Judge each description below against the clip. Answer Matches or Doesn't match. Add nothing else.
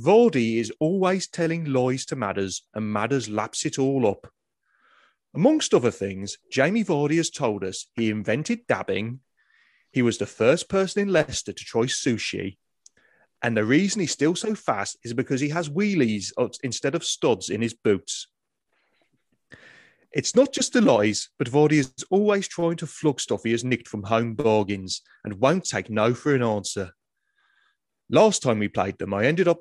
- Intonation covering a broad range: Matches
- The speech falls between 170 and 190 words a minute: Matches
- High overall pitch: Doesn't match